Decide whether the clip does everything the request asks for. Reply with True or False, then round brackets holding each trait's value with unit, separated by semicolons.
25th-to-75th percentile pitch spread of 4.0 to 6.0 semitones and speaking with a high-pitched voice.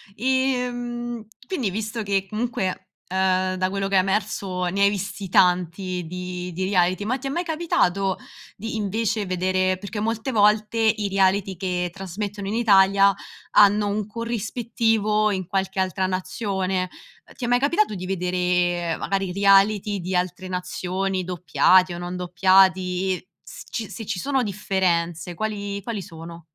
False (2.7 semitones; 195 Hz)